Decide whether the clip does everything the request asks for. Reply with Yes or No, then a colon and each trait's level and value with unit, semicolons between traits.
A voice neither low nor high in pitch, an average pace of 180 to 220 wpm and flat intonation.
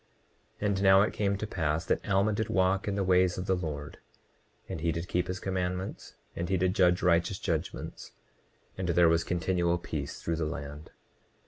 No: very low, 90 Hz; average, 195 wpm; narrow, 2.2 semitones